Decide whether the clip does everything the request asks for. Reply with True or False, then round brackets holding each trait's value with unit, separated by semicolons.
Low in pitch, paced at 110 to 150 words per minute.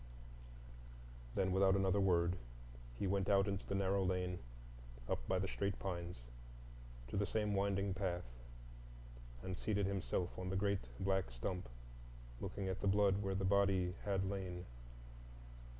True (95 Hz; 145 wpm)